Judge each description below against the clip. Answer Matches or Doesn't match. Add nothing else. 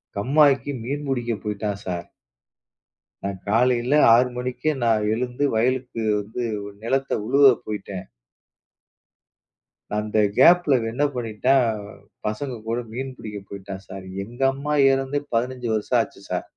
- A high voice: Doesn't match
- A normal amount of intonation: Matches